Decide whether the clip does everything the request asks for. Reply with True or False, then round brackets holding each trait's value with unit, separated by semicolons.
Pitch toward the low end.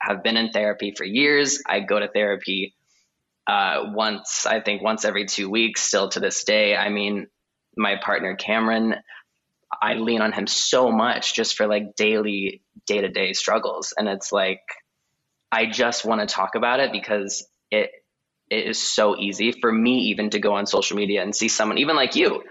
True (105 Hz)